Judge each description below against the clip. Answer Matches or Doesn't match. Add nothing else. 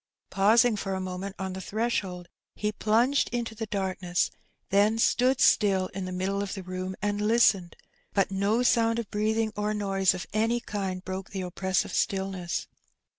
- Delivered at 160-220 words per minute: Matches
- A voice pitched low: Doesn't match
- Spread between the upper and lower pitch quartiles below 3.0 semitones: Matches